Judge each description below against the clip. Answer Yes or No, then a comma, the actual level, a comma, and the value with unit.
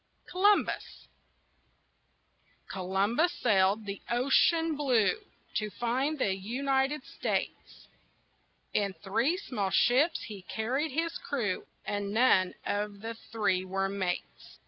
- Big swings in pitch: Yes, wide, 5.8 semitones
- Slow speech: Yes, slow, 110 wpm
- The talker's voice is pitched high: Yes, high, 225 Hz